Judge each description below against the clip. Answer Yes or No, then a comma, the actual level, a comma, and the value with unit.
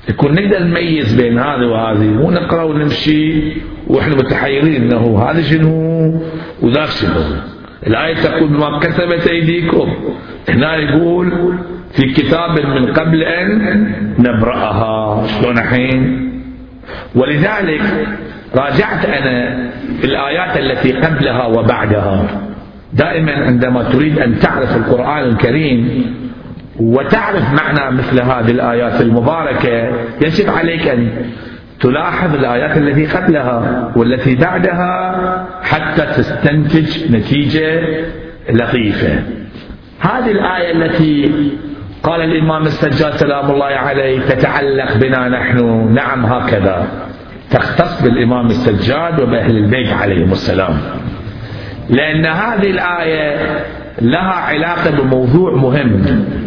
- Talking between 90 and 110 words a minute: Yes, average, 95 wpm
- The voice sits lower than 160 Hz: Yes, medium, 140 Hz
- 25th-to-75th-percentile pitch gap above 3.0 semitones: Yes, average, 5.1 semitones